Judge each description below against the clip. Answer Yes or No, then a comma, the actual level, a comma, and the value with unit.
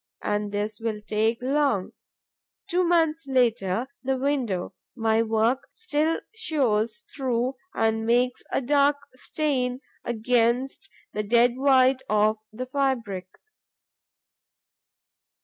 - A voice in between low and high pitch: No, high, 245 Hz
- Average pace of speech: No, slow, 105 wpm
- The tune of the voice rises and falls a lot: No, average, 3.8 semitones